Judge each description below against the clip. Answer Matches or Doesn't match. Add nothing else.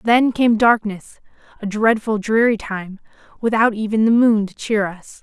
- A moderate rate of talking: Matches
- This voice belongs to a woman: Matches